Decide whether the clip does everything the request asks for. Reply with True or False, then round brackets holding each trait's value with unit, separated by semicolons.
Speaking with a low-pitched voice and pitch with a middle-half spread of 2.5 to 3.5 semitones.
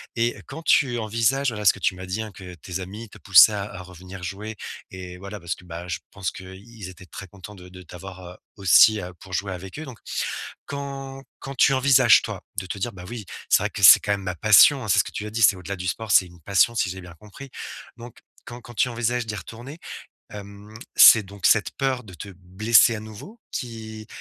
False (105 Hz; 4.0 semitones)